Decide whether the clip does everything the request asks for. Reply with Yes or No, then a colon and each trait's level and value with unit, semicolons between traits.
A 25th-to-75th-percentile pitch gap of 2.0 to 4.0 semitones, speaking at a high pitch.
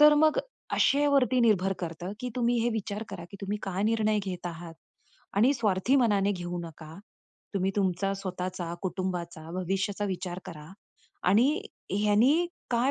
No: average, 4.6 semitones; high, 195 Hz